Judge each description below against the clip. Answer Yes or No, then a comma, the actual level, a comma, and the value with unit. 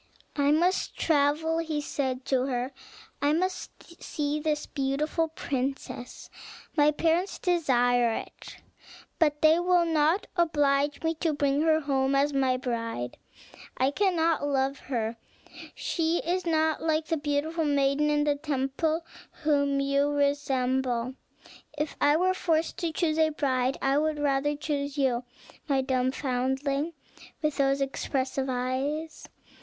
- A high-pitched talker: Yes, very high, 290 Hz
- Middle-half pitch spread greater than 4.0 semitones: No, average, 2.8 semitones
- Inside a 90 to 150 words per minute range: Yes, average, 140 wpm